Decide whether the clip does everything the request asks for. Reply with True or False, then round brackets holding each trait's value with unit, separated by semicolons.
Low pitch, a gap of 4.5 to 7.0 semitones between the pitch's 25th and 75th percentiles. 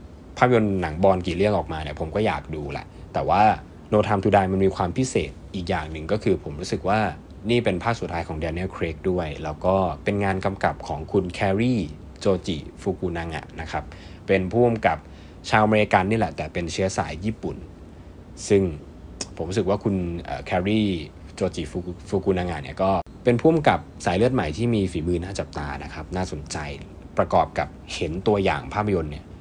False (90 Hz; 3.7 semitones)